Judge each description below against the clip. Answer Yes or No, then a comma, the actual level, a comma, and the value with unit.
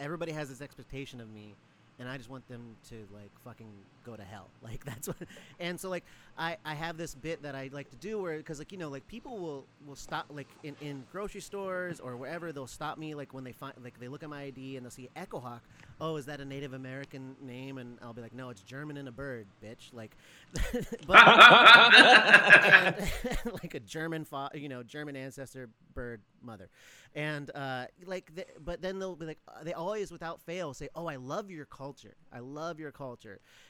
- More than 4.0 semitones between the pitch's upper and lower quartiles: Yes, average, 4.4 semitones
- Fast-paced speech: Yes, fast, 210 wpm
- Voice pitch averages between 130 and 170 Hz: Yes, medium, 140 Hz